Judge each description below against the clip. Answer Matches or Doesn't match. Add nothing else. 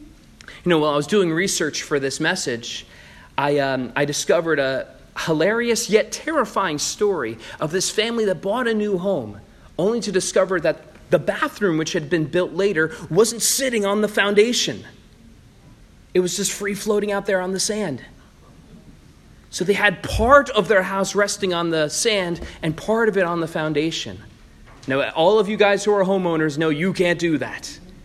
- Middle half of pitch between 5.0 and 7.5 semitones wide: Matches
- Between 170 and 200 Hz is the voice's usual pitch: Matches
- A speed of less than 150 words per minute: Doesn't match